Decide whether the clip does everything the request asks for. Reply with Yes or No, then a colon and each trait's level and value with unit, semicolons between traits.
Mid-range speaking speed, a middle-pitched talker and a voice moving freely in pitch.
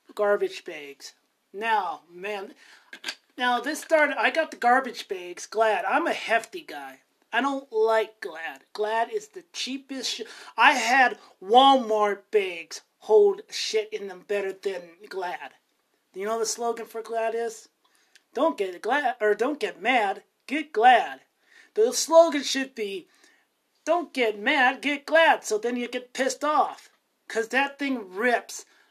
No: average, 150 wpm; very high, 270 Hz; wide, 8.2 semitones